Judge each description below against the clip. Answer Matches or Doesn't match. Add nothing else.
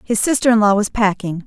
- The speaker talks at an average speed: Doesn't match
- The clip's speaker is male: Doesn't match